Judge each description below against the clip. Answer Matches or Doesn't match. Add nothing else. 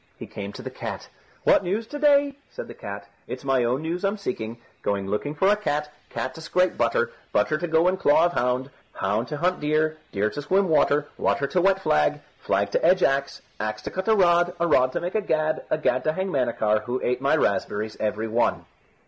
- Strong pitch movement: Matches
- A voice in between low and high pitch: Matches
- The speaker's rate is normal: Doesn't match